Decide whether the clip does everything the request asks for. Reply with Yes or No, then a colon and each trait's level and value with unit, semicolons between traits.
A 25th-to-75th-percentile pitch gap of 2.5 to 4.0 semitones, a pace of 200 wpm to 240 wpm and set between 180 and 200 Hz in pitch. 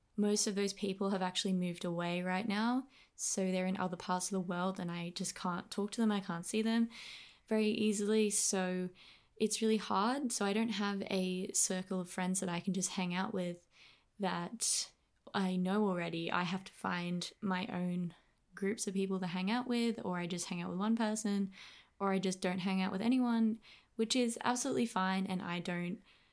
Yes: average, 2.8 semitones; fast, 205 wpm; high, 190 Hz